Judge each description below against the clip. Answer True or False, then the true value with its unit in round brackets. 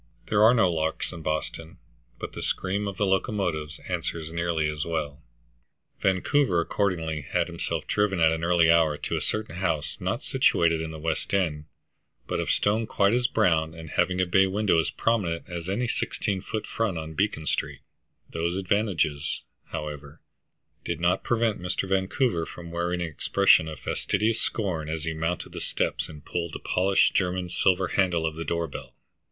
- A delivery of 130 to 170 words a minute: False (180 wpm)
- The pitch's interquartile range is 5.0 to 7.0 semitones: False (3.3 semitones)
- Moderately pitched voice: False (85 Hz)